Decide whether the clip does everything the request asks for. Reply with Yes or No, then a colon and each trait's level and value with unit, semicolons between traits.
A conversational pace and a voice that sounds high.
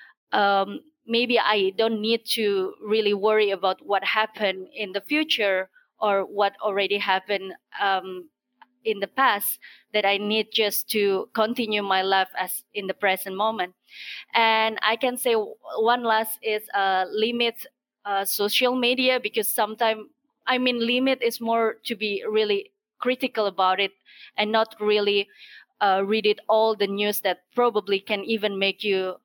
Yes: average, 155 wpm; high, 215 Hz